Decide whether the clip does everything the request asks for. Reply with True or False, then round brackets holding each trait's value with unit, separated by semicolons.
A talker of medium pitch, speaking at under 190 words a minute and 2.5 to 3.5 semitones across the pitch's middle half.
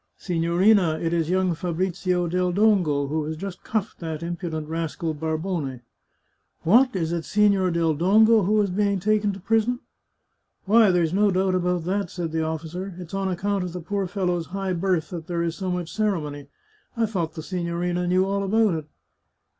False (180 Hz; 195 wpm; 3.1 semitones)